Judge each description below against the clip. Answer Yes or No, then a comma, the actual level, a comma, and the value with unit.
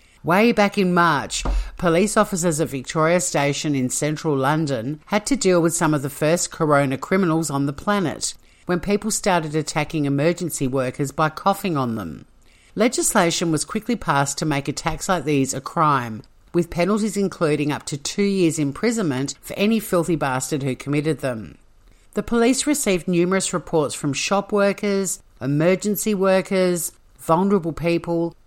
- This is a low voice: No, medium, 165 Hz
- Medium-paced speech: Yes, average, 155 wpm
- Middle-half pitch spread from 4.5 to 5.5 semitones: Yes, average, 5.1 semitones